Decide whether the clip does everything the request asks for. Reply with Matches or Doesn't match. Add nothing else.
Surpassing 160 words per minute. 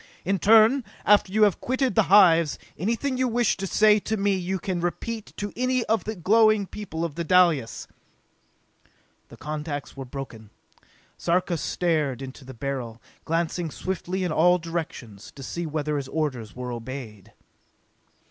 Doesn't match